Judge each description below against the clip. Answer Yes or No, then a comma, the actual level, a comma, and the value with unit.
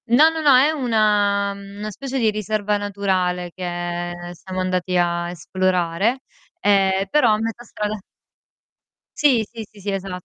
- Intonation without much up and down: No, average, 3.4 semitones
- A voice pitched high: Yes, high, 200 Hz